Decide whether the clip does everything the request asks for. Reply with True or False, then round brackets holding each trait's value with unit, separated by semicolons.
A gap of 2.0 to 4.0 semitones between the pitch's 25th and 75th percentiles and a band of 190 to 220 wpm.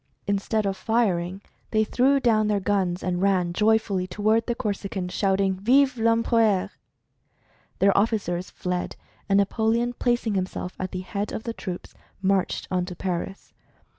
False (3.1 semitones; 145 wpm)